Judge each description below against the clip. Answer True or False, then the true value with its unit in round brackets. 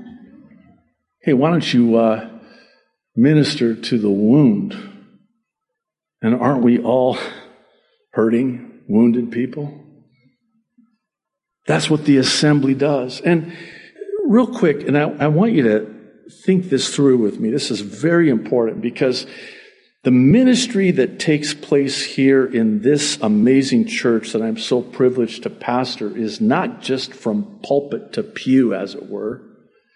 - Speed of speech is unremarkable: False (130 wpm)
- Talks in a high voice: False (140 Hz)